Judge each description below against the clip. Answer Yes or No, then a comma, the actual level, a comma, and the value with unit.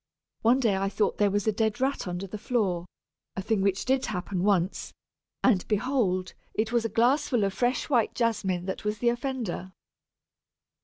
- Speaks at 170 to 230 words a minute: Yes, average, 175 wpm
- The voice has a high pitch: Yes, high, 210 Hz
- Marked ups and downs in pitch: No, average, 3.9 semitones